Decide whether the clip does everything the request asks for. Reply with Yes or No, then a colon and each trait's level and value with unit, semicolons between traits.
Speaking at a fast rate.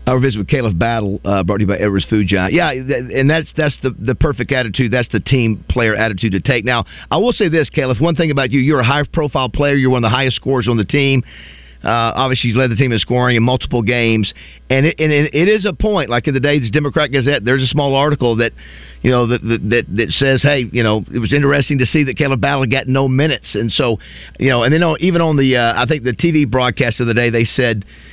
Yes: fast, 270 wpm